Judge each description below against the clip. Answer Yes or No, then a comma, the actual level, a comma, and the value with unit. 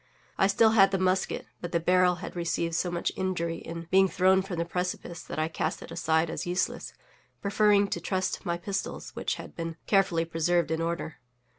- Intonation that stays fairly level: Yes, narrow, 2.3 semitones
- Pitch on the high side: No, medium, 175 Hz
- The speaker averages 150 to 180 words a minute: No, average, 195 wpm